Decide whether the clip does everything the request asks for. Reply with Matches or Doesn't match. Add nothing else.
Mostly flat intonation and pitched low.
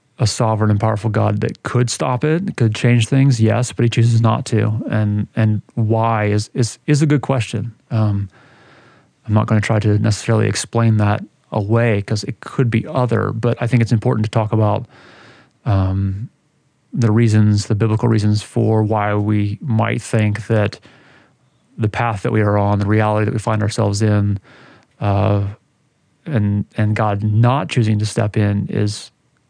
Matches